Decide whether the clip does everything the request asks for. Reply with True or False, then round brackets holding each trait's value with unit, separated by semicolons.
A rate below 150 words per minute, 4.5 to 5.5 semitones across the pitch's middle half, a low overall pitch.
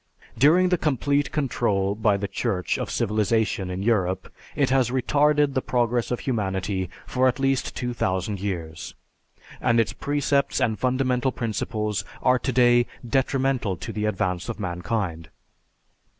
True (135 wpm; 5.0 semitones; 115 Hz)